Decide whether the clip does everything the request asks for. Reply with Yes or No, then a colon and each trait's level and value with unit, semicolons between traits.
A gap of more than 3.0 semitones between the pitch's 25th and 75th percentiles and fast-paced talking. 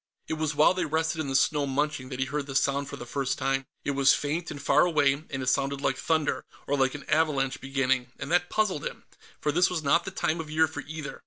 No: average, 2.7 semitones; fast, 255 wpm